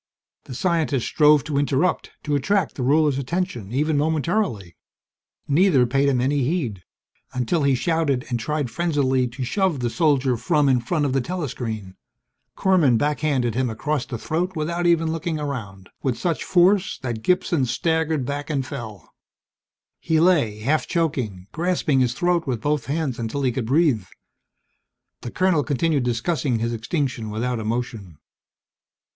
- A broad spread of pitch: No, average, 4.8 semitones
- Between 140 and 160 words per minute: Yes, average, 150 wpm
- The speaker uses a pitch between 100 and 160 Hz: Yes, medium, 140 Hz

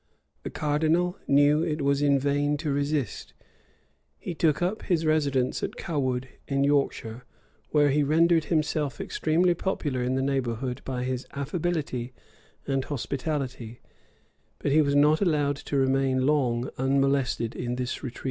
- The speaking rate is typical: Yes, average, 145 wpm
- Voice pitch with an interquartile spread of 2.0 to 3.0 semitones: Yes, average, 2.7 semitones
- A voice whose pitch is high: No, medium, 140 Hz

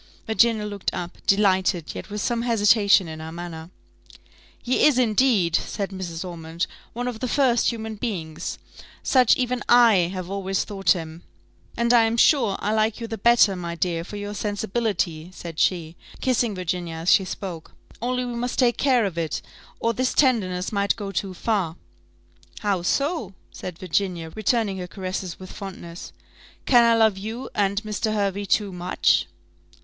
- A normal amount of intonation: Yes, average, 4.3 semitones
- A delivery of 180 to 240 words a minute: No, average, 170 wpm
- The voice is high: Yes, high, 200 Hz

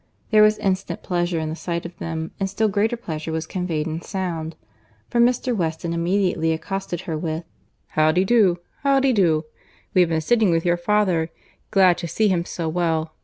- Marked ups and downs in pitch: No, average, 3.5 semitones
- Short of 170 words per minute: No, average, 175 wpm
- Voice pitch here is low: No, medium, 175 Hz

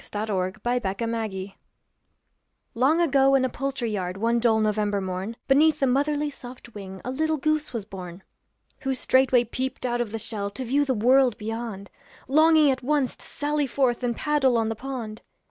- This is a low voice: No, high, 245 Hz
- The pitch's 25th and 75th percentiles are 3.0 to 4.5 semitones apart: Yes, average, 4.2 semitones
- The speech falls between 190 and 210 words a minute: Yes, average, 195 wpm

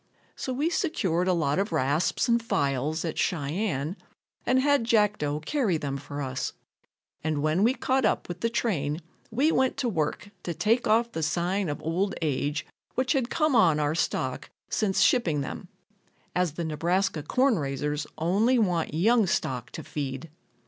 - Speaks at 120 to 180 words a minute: Yes, average, 170 wpm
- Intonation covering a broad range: Yes, wide, 7.4 semitones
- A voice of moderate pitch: Yes, medium, 175 Hz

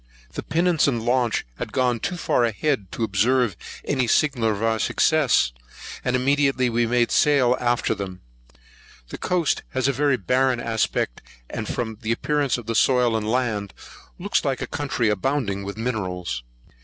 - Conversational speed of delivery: Yes, average, 165 wpm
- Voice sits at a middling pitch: No, low, 120 Hz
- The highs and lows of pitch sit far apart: No, average, 3.2 semitones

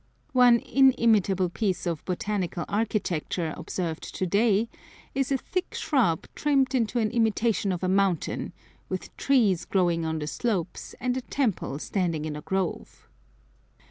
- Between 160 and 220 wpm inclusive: No, average, 140 wpm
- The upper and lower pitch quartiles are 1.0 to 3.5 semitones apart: No, wide, 5.5 semitones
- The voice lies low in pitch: No, high, 200 Hz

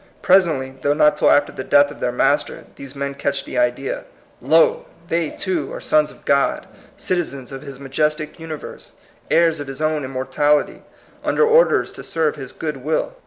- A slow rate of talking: No, average, 180 wpm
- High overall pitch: No, medium, 145 Hz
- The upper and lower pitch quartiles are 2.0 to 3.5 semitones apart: Yes, average, 2.8 semitones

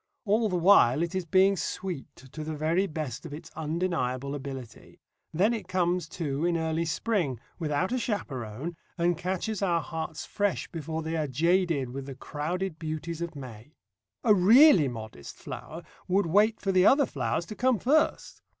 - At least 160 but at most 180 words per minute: Yes, average, 170 wpm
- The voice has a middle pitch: Yes, medium, 165 Hz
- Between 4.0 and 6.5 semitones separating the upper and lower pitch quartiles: Yes, average, 4.4 semitones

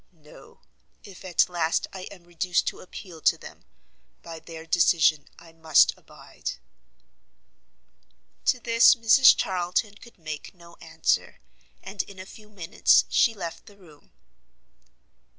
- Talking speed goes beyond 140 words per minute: No, slow, 135 wpm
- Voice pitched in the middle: Yes, medium, 180 Hz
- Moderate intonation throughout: Yes, average, 3.6 semitones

